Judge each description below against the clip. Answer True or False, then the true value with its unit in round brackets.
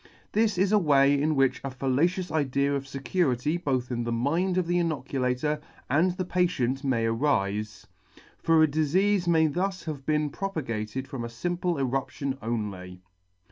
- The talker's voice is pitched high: False (140 Hz)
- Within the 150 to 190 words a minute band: True (160 wpm)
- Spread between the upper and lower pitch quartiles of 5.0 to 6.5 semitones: True (5.4 semitones)